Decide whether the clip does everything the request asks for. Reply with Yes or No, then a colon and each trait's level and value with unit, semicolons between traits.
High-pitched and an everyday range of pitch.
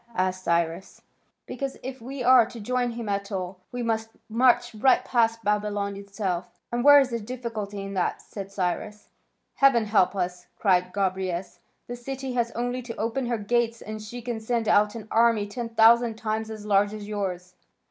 Yes: high, 220 Hz; average, 3.2 semitones